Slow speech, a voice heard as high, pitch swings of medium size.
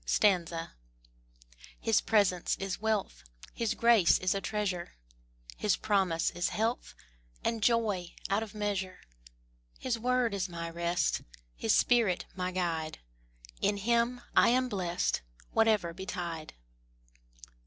Yes: slow, 115 wpm; high, 200 Hz; average, 4.1 semitones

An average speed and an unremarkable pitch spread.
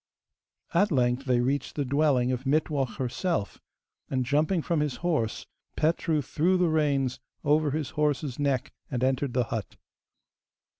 Yes: average, 145 wpm; average, 3.4 semitones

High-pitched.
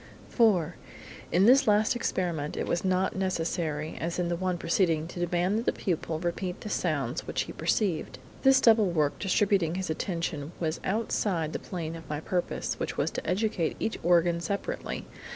No: medium, 175 Hz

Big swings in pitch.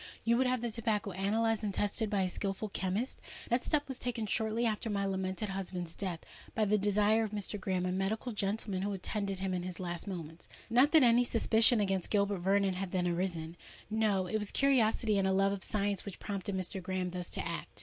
No: average, 2.7 semitones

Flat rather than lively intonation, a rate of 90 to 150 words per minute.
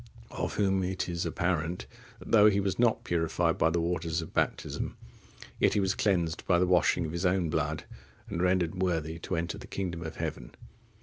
No: narrow, 2.3 semitones; average, 195 wpm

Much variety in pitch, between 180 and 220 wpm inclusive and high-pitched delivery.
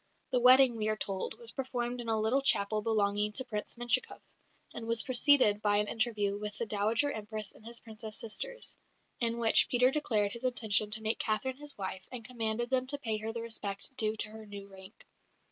No: average, 2.8 semitones; fast, 205 wpm; high, 220 Hz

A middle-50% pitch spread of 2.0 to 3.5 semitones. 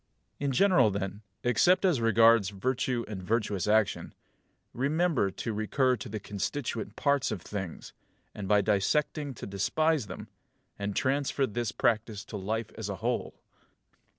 No: average, 4.5 semitones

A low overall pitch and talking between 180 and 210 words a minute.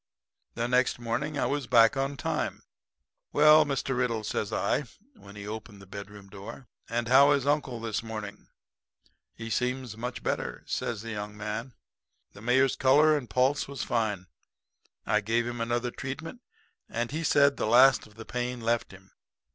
No: low, 120 Hz; average, 170 wpm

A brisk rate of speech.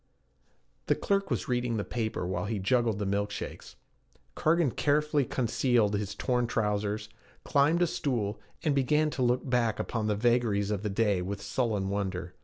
No: average, 170 wpm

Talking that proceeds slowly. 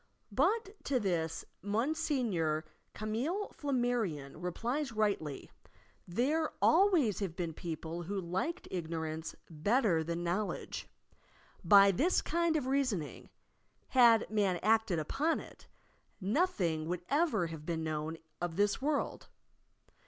Yes: slow, 115 wpm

